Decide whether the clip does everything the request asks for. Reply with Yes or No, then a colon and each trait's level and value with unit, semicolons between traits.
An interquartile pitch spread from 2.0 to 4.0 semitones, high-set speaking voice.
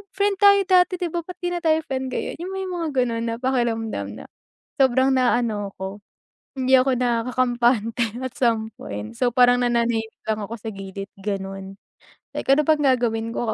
Yes: average, 3.3 semitones; high, 240 Hz